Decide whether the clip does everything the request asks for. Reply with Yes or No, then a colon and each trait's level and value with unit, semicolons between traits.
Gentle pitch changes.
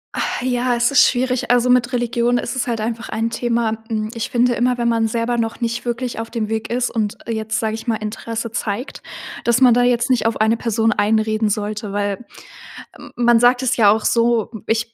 Yes: narrow, 1.7 semitones